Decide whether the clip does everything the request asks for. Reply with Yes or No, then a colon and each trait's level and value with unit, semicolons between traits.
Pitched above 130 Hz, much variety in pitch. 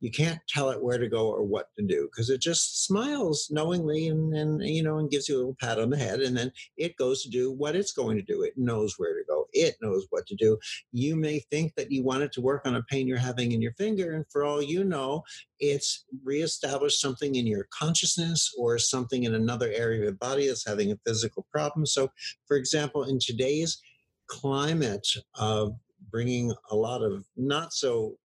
No: medium, 140 Hz; average, 4.3 semitones